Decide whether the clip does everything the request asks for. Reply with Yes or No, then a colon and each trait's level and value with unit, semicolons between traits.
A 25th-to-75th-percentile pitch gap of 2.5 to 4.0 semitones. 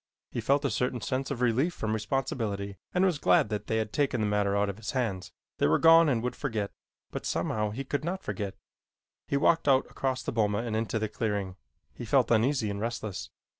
No: average, 4.6 semitones